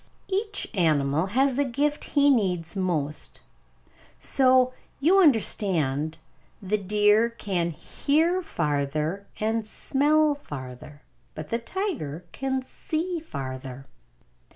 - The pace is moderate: No, slow, 105 wpm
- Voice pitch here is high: Yes, high, 210 Hz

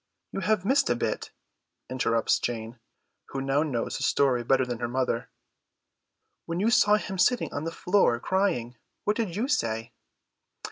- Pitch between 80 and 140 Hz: Yes, low, 135 Hz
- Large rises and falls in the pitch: Yes, wide, 8.9 semitones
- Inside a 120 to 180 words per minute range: Yes, average, 160 wpm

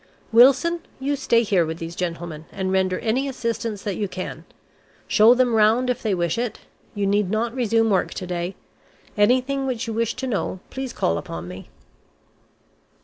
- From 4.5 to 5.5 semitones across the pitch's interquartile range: Yes, average, 5.1 semitones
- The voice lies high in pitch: Yes, high, 220 Hz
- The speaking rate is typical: Yes, average, 175 wpm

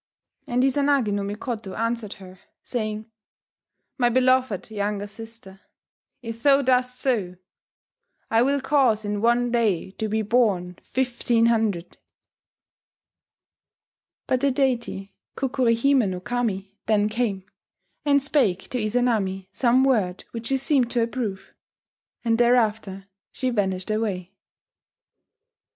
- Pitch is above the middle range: Yes, high, 230 Hz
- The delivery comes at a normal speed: No, slow, 120 wpm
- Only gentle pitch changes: No, average, 3.7 semitones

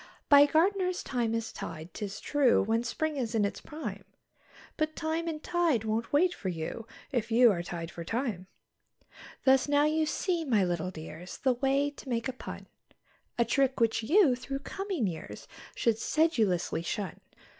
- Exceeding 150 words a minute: Yes, average, 170 wpm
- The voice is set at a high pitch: Yes, high, 245 Hz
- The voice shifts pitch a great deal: Yes, wide, 6.2 semitones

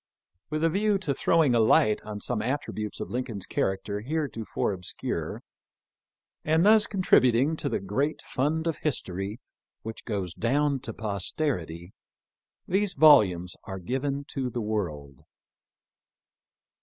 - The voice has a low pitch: Yes, low, 120 Hz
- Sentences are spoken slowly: Yes, slow, 130 wpm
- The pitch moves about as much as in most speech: No, wide, 6.9 semitones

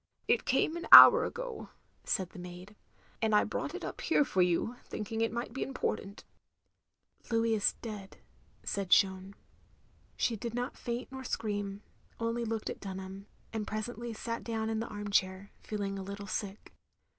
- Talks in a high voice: Yes, high, 215 Hz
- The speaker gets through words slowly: No, average, 180 wpm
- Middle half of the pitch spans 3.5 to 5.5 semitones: No, average, 3.0 semitones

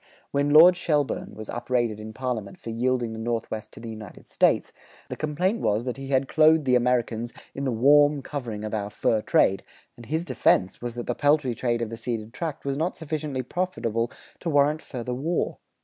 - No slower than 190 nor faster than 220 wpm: Yes, average, 195 wpm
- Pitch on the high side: No, low, 125 Hz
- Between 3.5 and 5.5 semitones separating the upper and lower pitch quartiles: Yes, average, 4.4 semitones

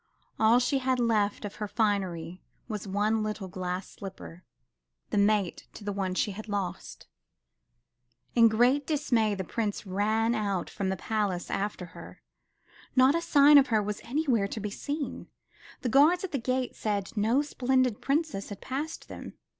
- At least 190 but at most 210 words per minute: No, average, 165 wpm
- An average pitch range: Yes, average, 4.4 semitones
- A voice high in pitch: Yes, high, 215 Hz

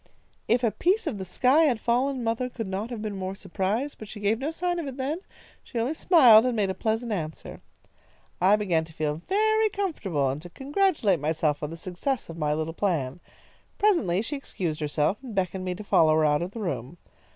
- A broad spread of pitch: Yes, wide, 7.6 semitones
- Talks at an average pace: No, fast, 215 wpm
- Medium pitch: No, high, 210 Hz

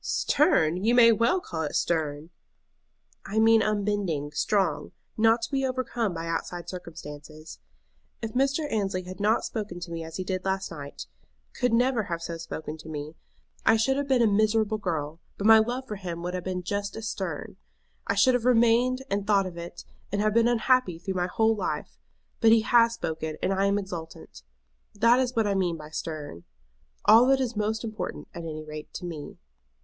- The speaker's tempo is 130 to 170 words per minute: No, average, 195 wpm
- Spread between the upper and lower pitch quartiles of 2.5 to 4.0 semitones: No, average, 5.2 semitones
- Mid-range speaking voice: No, high, 200 Hz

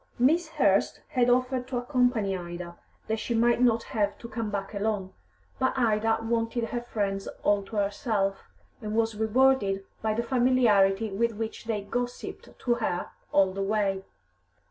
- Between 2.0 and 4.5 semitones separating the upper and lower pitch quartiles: Yes, average, 3.3 semitones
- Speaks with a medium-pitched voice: No, high, 220 Hz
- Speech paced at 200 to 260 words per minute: No, average, 160 wpm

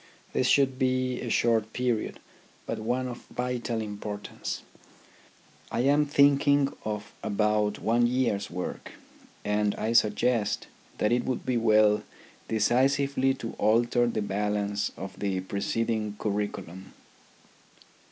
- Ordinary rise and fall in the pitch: Yes, average, 3.3 semitones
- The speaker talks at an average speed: No, slow, 125 wpm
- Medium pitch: No, low, 115 Hz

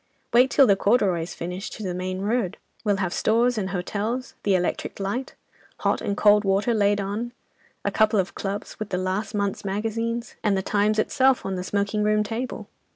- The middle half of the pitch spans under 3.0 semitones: Yes, narrow, 2.6 semitones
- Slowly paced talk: No, average, 190 wpm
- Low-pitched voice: No, high, 205 Hz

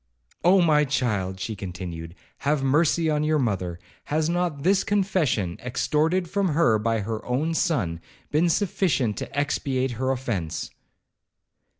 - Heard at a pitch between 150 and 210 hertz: No, medium, 140 Hz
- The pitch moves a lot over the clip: Yes, wide, 7.2 semitones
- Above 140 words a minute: No, slow, 135 wpm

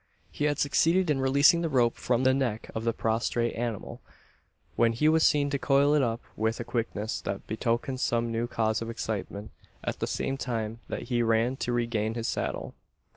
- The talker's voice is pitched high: No, low, 120 Hz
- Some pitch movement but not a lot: Yes, average, 3.2 semitones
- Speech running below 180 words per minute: No, average, 195 wpm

